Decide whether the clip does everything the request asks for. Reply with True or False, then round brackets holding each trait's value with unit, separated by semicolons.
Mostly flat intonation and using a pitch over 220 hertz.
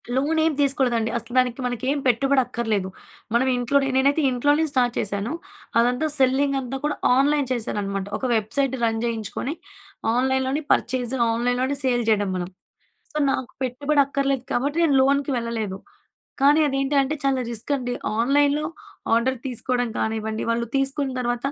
False (3.0 semitones; 255 Hz)